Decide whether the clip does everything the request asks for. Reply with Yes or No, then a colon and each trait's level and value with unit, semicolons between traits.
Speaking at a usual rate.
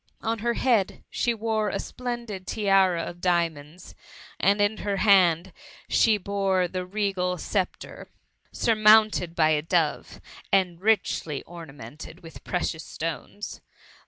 No: slow, 125 wpm